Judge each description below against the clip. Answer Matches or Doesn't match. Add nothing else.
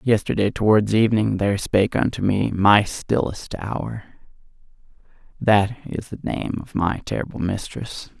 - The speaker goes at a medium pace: Doesn't match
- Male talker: Matches